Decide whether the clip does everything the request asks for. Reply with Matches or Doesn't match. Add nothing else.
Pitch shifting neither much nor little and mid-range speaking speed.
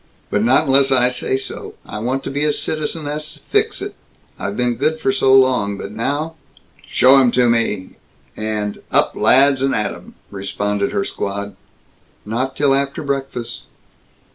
Matches